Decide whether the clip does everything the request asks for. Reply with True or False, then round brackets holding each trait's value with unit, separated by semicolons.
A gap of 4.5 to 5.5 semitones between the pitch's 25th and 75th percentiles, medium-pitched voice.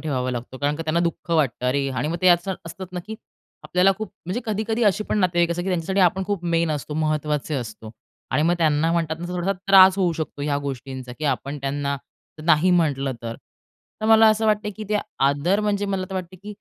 True (4.9 semitones; 170 Hz)